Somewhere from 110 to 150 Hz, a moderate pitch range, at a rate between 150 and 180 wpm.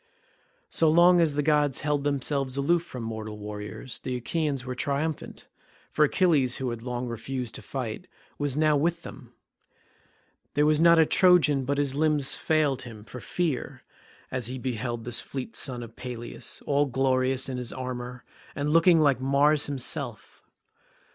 Yes: low, 135 Hz; average, 3.3 semitones; average, 160 wpm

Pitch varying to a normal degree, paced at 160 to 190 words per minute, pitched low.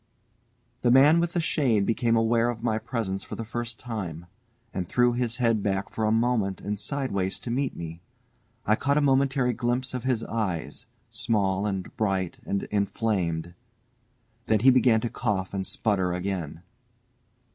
Yes: average, 4.1 semitones; average, 165 wpm; low, 110 Hz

